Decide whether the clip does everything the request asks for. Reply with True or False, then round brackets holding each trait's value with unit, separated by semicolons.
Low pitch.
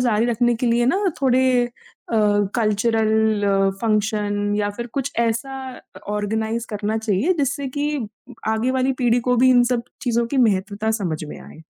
False (230 Hz)